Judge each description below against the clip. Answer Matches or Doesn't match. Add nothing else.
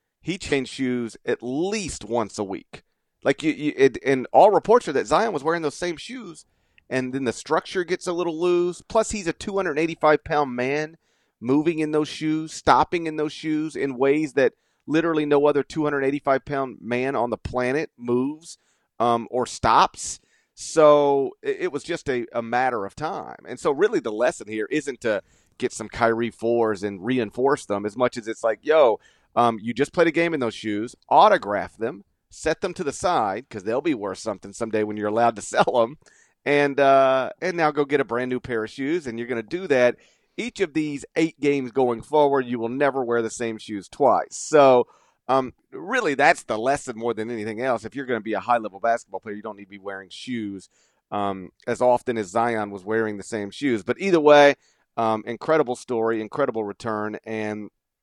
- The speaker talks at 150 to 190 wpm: Doesn't match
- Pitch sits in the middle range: Doesn't match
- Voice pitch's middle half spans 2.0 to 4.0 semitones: Doesn't match